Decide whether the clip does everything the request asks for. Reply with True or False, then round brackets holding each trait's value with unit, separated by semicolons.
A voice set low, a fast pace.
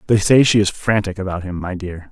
True (95 Hz; 255 wpm)